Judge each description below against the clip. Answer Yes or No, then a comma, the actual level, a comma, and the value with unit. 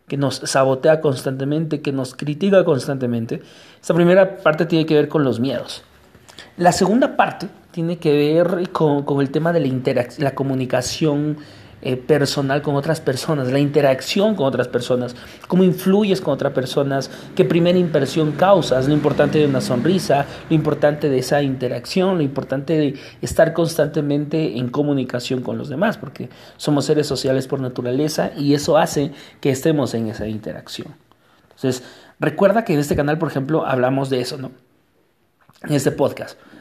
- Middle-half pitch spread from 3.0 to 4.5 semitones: Yes, average, 3.4 semitones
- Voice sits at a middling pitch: Yes, medium, 145 Hz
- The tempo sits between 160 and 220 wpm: Yes, average, 165 wpm